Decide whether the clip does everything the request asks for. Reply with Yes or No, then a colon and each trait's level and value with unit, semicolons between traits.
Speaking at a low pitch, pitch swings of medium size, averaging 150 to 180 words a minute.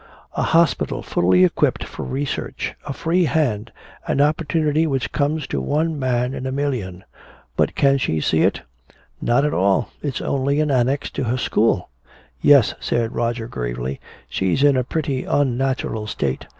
Yes: low, 130 Hz; average, 4.3 semitones; average, 160 wpm